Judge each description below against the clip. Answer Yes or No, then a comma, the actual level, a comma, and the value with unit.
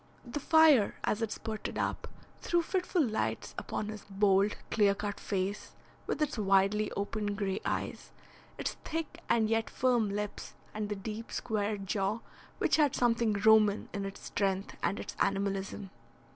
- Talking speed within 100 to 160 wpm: Yes, average, 155 wpm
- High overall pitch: Yes, high, 210 Hz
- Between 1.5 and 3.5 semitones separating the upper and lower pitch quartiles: Yes, narrow, 2.4 semitones